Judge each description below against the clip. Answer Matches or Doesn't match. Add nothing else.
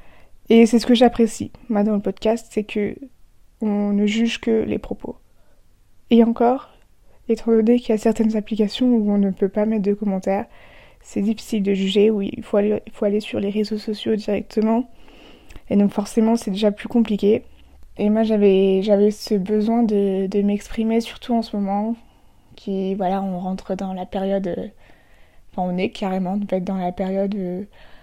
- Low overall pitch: Doesn't match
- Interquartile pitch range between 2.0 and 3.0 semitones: Matches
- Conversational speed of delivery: Matches